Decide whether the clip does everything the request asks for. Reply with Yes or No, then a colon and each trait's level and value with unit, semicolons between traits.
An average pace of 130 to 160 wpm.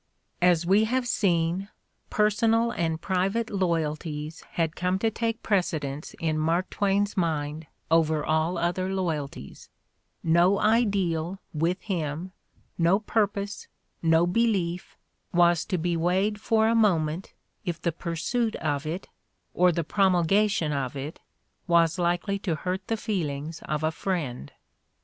Yes: slow, 135 wpm